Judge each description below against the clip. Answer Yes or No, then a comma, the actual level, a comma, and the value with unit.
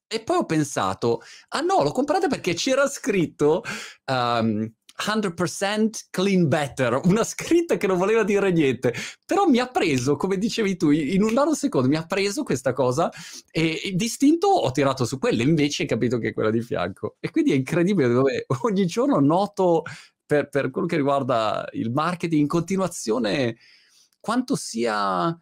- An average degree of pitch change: No, wide, 7.3 semitones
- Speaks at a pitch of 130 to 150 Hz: No, medium, 175 Hz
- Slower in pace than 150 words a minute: No, fast, 170 wpm